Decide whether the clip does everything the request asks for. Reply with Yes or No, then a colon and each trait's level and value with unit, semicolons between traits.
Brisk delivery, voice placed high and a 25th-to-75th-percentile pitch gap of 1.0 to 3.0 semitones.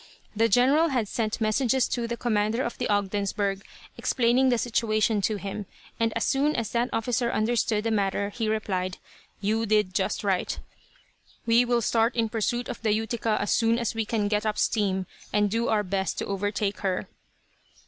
No: average, 180 wpm; high, 220 Hz; narrow, 2.4 semitones